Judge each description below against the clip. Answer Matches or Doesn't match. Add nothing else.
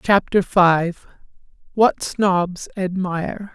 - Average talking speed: Doesn't match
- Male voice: Matches